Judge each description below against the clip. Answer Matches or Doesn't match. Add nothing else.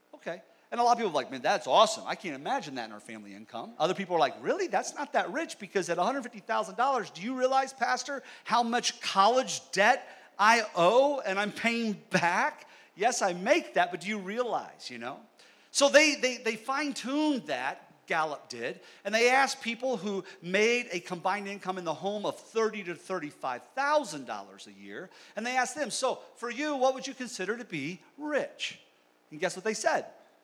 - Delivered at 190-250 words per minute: Matches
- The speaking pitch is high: Matches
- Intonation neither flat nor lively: Doesn't match